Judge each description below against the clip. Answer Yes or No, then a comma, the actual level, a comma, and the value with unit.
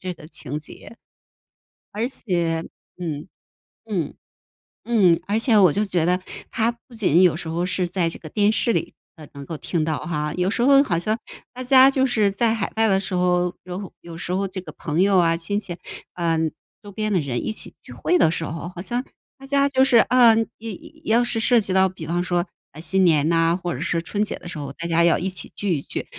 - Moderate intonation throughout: Yes, average, 4.7 semitones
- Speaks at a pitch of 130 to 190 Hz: Yes, medium, 185 Hz